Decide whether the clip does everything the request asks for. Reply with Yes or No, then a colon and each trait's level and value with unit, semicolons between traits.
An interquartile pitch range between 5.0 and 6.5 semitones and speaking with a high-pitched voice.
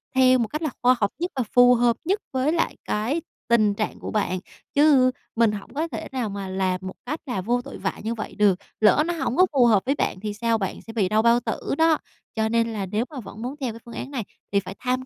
No: average, 3.8 semitones; high, 235 Hz